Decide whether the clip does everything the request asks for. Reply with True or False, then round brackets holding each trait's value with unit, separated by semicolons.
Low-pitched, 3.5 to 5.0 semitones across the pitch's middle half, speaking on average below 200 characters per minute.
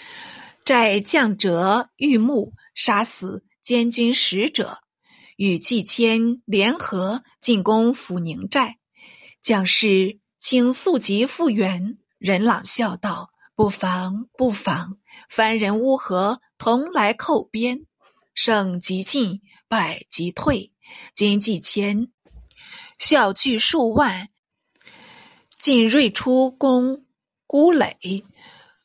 False (225 Hz; 4.3 semitones; 135 characters per minute)